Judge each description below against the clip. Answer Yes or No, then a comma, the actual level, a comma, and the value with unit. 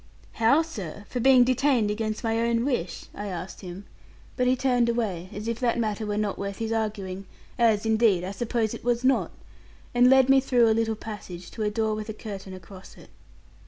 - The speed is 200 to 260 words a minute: Yes, fast, 205 wpm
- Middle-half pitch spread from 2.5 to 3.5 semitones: Yes, average, 3.0 semitones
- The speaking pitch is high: Yes, high, 220 Hz